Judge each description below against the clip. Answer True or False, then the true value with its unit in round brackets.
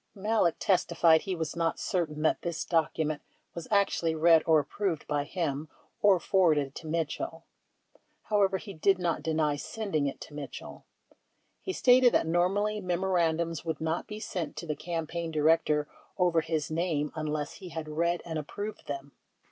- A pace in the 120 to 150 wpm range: False (165 wpm)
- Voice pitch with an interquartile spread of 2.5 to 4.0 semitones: True (3.0 semitones)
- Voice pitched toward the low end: False (165 Hz)